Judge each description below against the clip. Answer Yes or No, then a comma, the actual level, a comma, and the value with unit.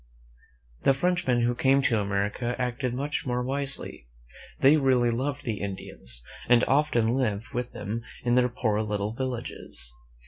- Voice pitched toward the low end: Yes, low, 125 Hz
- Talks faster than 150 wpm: No, average, 145 wpm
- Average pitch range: Yes, average, 3.4 semitones